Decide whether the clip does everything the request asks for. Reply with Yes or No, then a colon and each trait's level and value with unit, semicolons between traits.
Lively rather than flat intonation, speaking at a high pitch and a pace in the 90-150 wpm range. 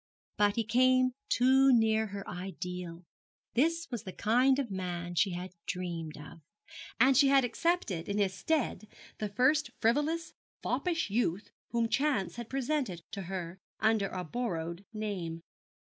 Yes: wide, 6.0 semitones; high, 215 Hz; average, 145 wpm